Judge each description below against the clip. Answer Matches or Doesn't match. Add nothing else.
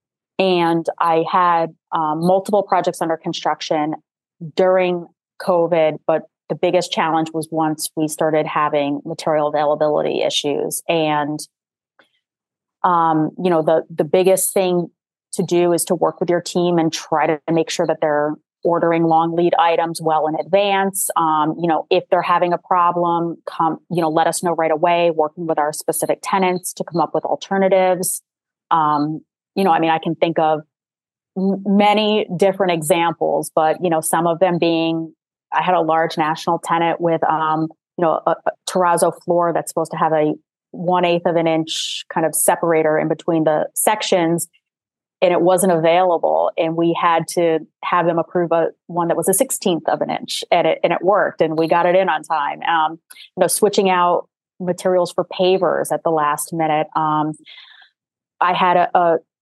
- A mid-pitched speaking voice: Matches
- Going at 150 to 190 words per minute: Matches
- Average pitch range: Doesn't match